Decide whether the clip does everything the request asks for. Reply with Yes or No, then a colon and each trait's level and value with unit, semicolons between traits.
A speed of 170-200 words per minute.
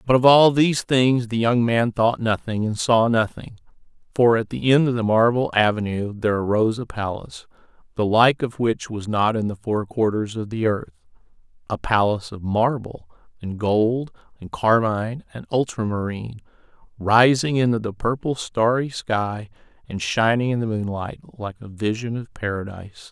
No: average, 160 wpm